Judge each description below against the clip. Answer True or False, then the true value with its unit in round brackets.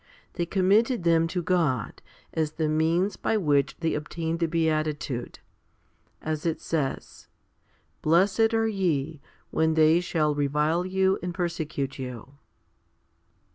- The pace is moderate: False (130 wpm)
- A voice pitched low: False (160 Hz)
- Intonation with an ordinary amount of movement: True (3.0 semitones)